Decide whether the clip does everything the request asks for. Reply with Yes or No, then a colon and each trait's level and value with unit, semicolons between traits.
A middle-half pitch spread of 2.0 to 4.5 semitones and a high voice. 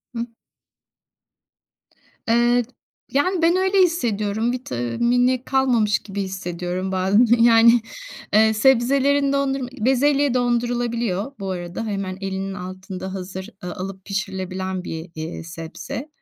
No: average, 5.0 semitones; high, 220 Hz